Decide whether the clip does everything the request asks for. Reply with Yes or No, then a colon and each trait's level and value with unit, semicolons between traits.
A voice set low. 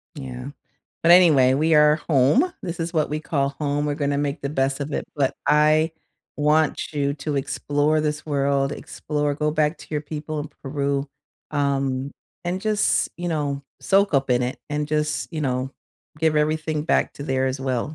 No: medium, 150 Hz